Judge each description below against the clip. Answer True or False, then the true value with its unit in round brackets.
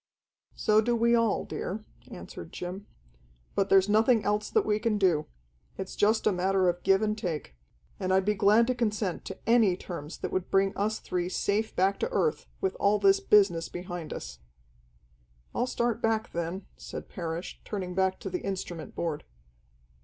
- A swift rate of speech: False (175 wpm)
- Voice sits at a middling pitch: False (200 Hz)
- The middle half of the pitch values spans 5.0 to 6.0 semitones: False (3.2 semitones)